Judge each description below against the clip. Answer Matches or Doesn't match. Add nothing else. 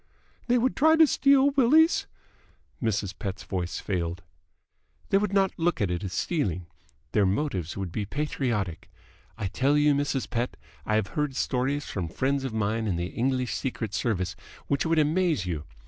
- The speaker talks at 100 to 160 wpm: Doesn't match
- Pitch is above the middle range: Doesn't match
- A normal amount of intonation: Doesn't match